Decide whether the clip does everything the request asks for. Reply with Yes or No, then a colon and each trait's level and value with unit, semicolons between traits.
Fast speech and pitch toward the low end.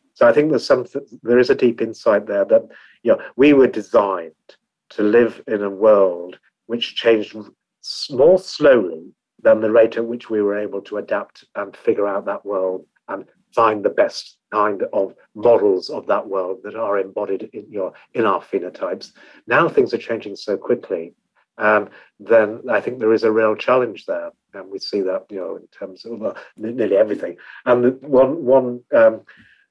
No: average, 180 wpm; low, 125 Hz